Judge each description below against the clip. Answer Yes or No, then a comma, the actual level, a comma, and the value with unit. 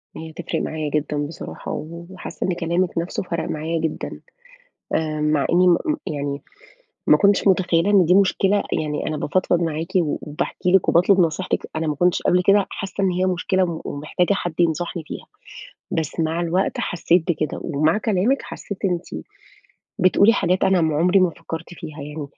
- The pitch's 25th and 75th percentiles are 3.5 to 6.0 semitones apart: No, average, 2.8 semitones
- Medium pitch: Yes, medium, 170 Hz